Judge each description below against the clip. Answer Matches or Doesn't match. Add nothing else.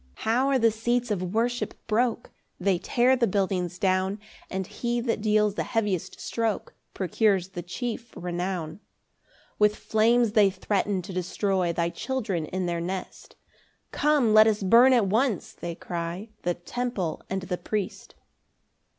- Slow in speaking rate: Doesn't match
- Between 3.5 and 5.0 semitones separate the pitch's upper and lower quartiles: Matches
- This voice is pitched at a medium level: Doesn't match